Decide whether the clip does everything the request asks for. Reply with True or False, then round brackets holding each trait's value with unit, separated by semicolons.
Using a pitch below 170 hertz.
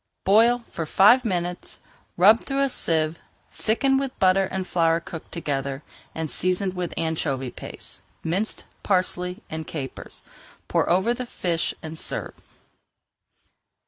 False (180 Hz)